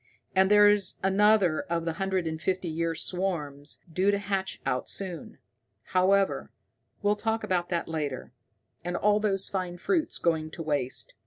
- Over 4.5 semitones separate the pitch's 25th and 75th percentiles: No, average, 3.3 semitones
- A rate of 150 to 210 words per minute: Yes, average, 155 wpm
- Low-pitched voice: No, medium, 185 Hz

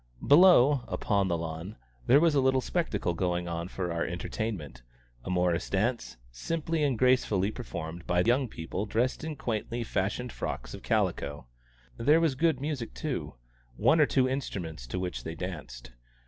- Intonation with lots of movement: Yes, wide, 7.2 semitones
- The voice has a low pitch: Yes, low, 105 Hz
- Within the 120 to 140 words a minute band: No, average, 160 wpm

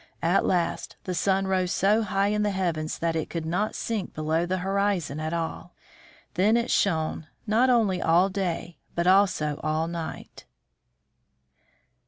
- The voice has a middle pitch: Yes, medium, 180 Hz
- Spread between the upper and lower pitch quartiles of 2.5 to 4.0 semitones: Yes, average, 3.4 semitones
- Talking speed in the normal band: Yes, average, 155 wpm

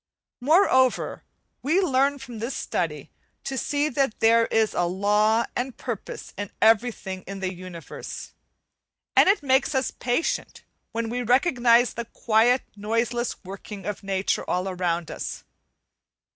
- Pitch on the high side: Yes, high, 230 Hz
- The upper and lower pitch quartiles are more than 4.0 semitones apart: Yes, average, 4.7 semitones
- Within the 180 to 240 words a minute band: No, slow, 135 wpm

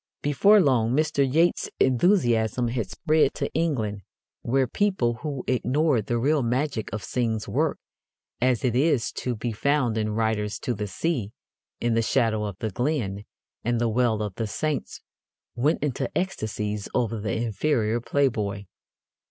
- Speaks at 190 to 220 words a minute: No, average, 150 wpm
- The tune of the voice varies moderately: Yes, average, 4.5 semitones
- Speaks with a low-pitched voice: Yes, low, 120 Hz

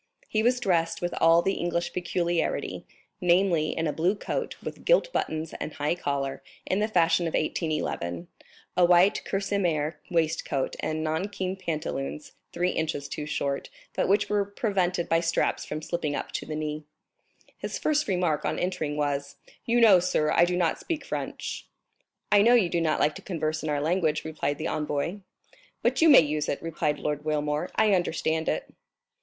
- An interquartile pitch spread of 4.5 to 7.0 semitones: No, average, 3.4 semitones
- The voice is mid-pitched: Yes, medium, 165 Hz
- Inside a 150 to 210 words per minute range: Yes, average, 175 wpm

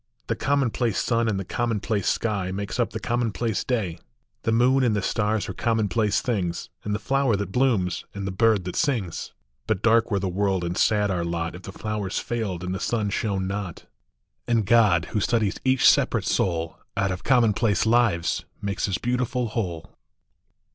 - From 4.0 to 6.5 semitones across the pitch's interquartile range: No, average, 3.6 semitones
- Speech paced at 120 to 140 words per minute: No, average, 180 wpm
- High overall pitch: No, low, 105 Hz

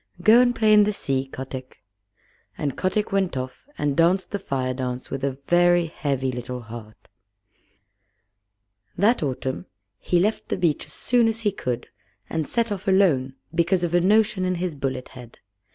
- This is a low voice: No, medium, 165 Hz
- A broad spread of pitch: Yes, wide, 7.0 semitones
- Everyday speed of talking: Yes, average, 170 wpm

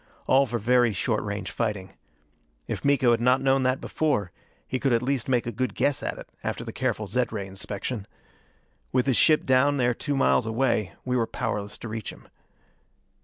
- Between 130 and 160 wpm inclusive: No, average, 195 wpm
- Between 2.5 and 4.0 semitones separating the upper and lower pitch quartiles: Yes, average, 3.4 semitones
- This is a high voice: No, low, 120 Hz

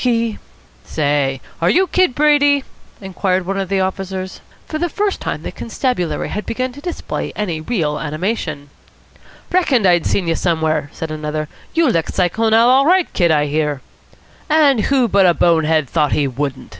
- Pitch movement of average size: No, wide, 8.5 semitones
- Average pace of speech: Yes, average, 180 wpm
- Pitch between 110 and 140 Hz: No, high, 190 Hz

